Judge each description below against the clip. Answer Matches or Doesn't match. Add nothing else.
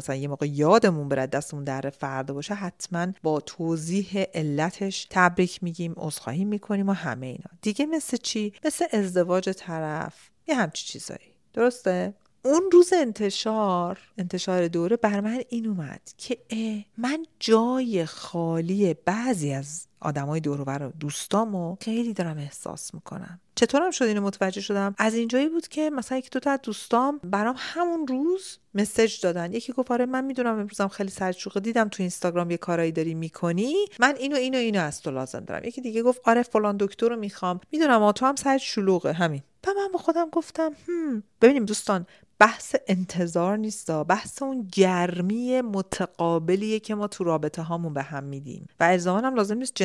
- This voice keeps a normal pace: Doesn't match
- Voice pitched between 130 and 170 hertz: Doesn't match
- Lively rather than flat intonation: Matches